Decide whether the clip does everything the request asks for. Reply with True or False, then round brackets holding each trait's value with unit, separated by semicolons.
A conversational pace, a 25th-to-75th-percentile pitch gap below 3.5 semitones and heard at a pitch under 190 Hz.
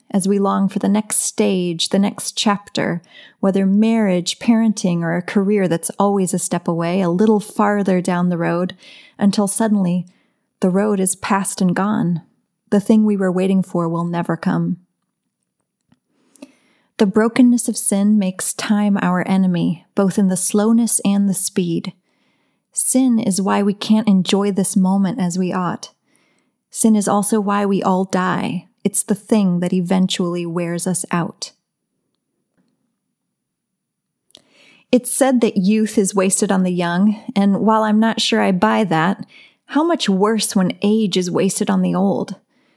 False (155 wpm; 2.7 semitones; 200 Hz)